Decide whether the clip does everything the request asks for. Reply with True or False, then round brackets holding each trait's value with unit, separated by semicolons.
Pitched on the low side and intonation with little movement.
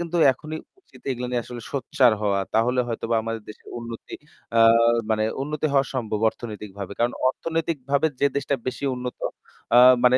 False (125 Hz; 3.8 semitones)